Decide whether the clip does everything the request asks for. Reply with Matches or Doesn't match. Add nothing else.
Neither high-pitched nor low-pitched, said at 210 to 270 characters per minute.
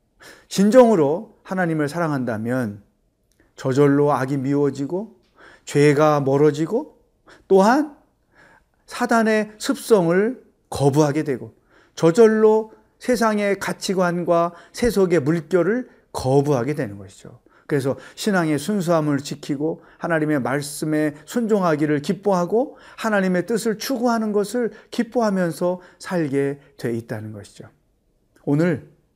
Matches